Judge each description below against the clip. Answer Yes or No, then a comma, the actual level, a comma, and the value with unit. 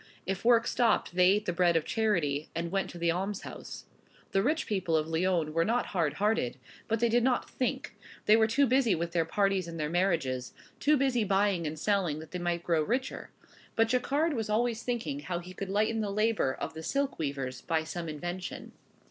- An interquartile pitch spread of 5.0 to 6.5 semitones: Yes, average, 5.3 semitones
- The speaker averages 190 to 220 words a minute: Yes, fast, 205 wpm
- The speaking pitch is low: No, high, 190 Hz